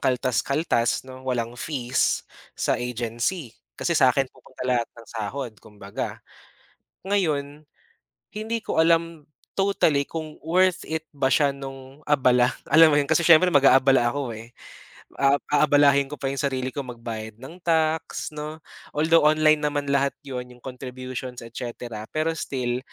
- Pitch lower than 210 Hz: Yes, medium, 140 Hz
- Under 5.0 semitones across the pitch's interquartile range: Yes, average, 3.7 semitones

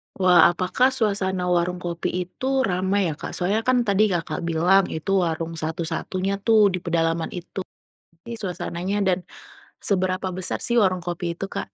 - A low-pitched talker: No, medium, 185 Hz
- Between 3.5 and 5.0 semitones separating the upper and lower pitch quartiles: No, narrow, 2.5 semitones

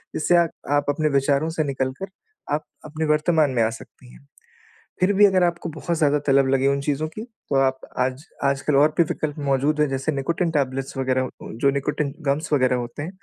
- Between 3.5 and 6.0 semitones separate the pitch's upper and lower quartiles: No, narrow, 2.6 semitones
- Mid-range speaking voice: Yes, medium, 145 Hz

